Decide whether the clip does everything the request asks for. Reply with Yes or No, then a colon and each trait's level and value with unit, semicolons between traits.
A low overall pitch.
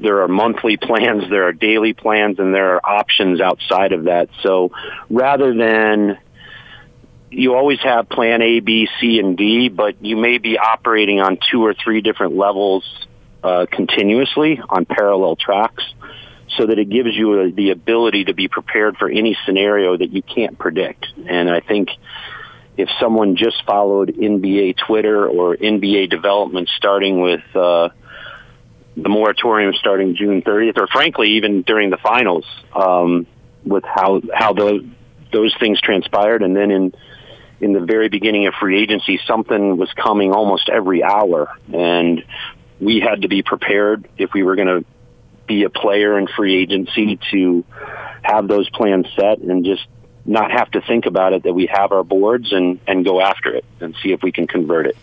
Yes: low, 100 Hz